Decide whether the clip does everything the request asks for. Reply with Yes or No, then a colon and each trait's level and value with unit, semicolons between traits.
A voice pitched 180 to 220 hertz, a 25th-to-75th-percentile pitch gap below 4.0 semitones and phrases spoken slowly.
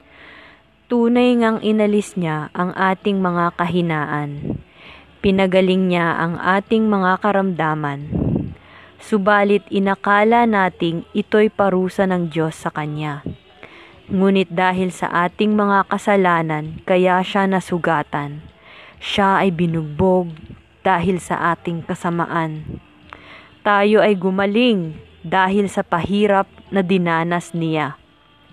Yes: medium, 185 Hz; average, 3.2 semitones; slow, 100 wpm